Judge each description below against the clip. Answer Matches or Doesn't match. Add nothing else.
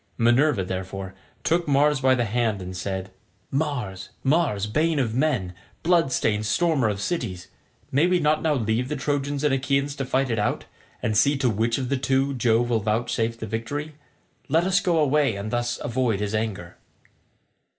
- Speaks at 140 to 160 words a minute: Doesn't match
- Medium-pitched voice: Doesn't match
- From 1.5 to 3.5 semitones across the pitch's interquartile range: Doesn't match